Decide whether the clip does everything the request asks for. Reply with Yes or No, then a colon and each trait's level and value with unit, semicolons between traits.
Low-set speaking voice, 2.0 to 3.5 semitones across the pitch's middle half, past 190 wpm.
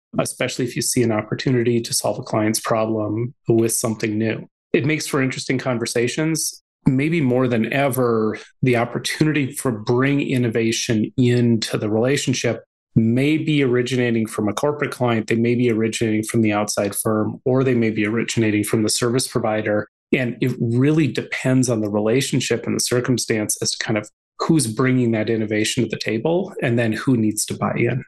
No: low, 120 Hz; average, 2.9 semitones; average, 175 wpm